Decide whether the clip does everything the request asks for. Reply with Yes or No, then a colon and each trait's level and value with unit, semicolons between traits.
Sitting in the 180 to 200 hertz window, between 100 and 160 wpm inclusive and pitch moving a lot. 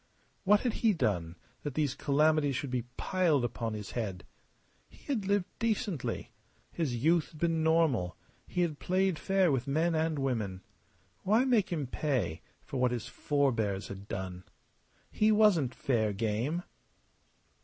No: medium, 145 Hz; average, 150 wpm; wide, 7.2 semitones